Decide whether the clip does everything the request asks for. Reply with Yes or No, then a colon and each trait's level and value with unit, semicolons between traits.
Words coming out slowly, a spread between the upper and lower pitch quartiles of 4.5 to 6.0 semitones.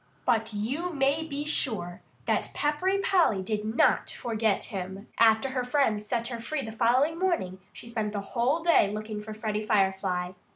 No: average, 170 wpm; average, 5.1 semitones